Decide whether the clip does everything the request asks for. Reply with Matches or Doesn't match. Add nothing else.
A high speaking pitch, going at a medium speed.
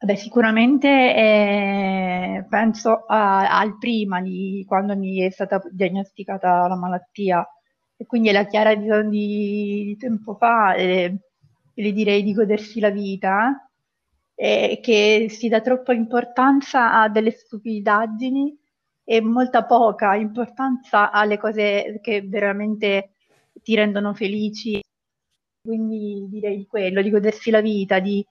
Matches